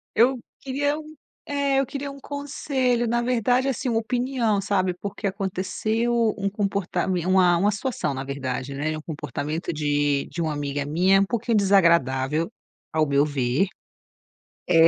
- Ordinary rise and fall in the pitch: No, wide, 7.6 semitones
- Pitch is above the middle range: Yes, high, 195 Hz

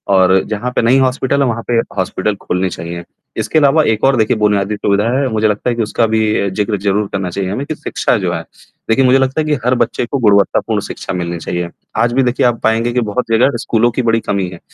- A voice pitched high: No, low, 110 Hz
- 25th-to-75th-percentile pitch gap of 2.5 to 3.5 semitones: No, average, 4.0 semitones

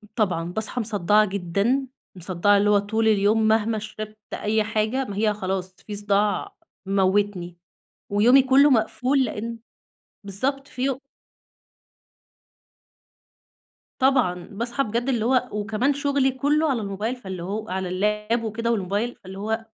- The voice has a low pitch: No, high, 215 Hz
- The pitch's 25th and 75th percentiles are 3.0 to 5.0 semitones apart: Yes, average, 3.6 semitones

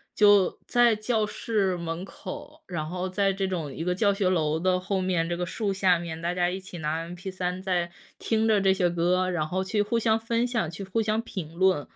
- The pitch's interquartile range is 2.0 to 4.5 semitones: Yes, average, 2.9 semitones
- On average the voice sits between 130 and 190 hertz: Yes, medium, 185 Hz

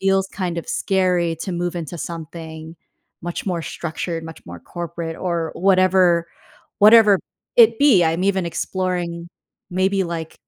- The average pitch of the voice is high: No, medium, 175 Hz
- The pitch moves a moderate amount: No, narrow, 2.2 semitones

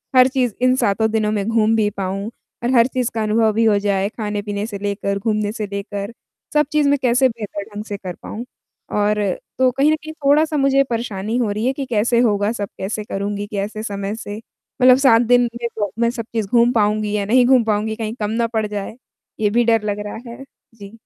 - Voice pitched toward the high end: Yes, high, 220 Hz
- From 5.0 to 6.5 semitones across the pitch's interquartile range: No, average, 2.8 semitones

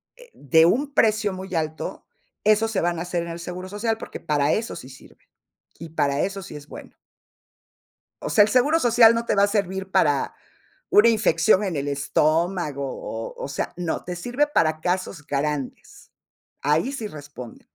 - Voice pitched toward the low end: No, medium, 180 Hz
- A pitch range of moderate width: No, wide, 6.2 semitones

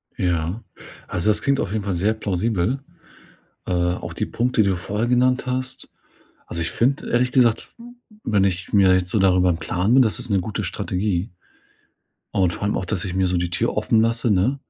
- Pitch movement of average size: Yes, average, 4.4 semitones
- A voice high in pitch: No, low, 100 Hz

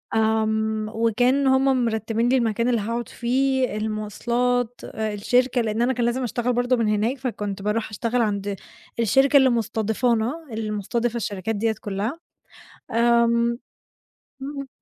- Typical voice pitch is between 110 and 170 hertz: No, high, 235 Hz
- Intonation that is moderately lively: No, narrow, 2.2 semitones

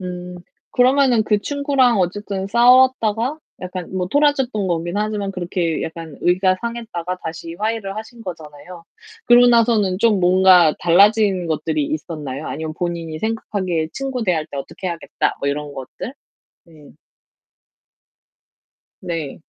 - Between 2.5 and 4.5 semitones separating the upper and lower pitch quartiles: No, wide, 5.4 semitones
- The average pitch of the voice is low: No, medium, 185 Hz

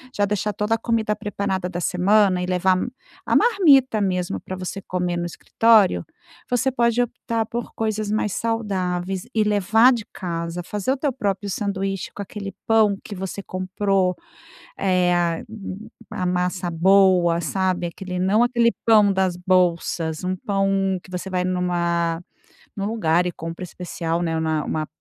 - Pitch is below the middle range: No, high, 190 Hz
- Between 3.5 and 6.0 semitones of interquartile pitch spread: No, average, 2.9 semitones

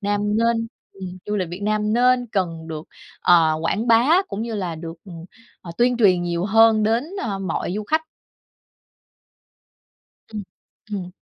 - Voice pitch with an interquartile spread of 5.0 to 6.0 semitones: No, average, 4.4 semitones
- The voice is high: Yes, high, 205 Hz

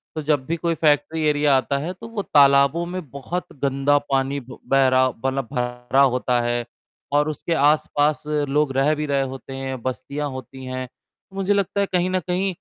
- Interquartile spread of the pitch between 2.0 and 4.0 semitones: Yes, average, 2.9 semitones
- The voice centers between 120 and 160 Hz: Yes, medium, 140 Hz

